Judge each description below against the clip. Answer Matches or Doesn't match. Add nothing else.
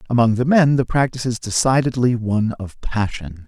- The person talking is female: Doesn't match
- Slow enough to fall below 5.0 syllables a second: Doesn't match